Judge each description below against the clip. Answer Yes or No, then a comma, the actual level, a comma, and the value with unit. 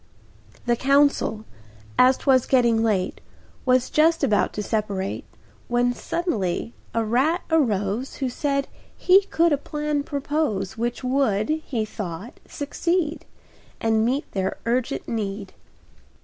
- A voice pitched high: Yes, high, 245 Hz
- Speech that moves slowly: Yes, slow, 120 wpm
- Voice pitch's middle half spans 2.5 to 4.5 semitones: No, average, 5.0 semitones